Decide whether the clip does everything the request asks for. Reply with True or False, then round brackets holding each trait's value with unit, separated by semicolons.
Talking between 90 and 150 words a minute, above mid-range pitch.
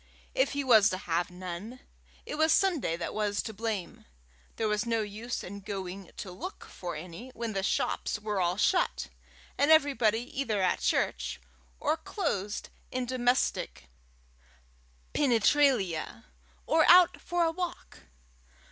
True (140 wpm; 220 Hz)